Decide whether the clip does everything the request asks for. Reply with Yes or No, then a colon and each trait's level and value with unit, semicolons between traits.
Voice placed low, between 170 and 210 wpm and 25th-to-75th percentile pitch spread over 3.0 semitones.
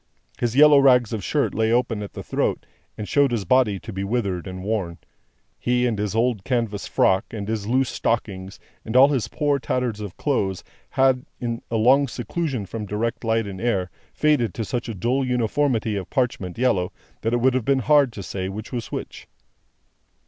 Yes: low, 115 Hz; average, 200 wpm; average, 3.9 semitones